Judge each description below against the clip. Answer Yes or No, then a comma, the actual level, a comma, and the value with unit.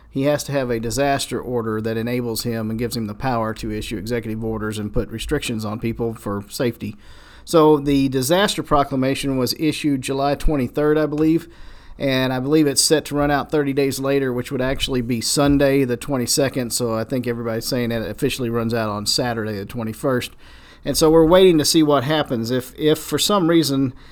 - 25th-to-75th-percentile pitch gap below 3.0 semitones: No, average, 4.0 semitones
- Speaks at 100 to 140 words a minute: No, average, 200 wpm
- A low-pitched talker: Yes, low, 130 Hz